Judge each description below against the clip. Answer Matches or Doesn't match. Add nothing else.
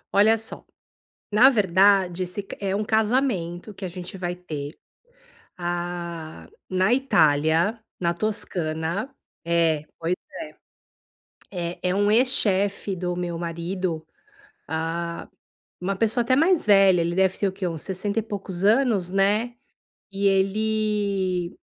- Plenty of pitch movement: Doesn't match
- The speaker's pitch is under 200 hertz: Matches